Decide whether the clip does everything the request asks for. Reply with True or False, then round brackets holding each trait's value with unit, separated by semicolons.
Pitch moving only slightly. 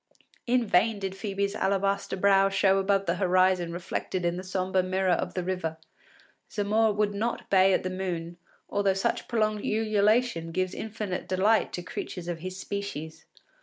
True (1.8 semitones)